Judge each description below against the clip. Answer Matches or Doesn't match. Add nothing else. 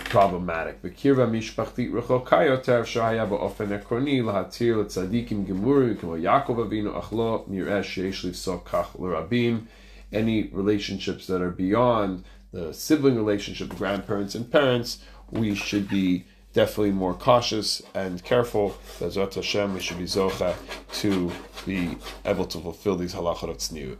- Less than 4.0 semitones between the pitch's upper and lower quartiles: Matches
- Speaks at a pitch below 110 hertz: Matches